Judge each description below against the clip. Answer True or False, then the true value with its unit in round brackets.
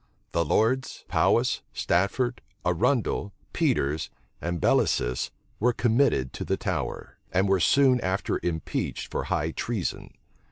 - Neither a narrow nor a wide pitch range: False (6.3 semitones)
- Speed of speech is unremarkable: False (120 wpm)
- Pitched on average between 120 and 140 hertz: False (95 Hz)